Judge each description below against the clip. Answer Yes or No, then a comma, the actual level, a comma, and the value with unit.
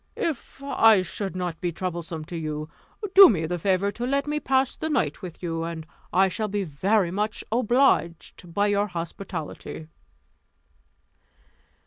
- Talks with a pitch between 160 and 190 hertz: Yes, medium, 185 Hz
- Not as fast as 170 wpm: Yes, average, 150 wpm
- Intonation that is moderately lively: Yes, average, 4.7 semitones